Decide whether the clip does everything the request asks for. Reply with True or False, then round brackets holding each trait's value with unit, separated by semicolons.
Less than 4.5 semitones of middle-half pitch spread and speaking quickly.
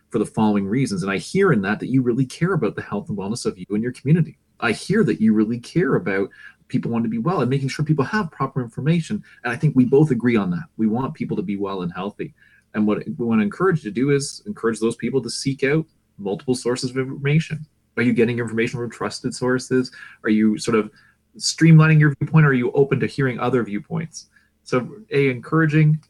False (4.8 semitones; 235 wpm)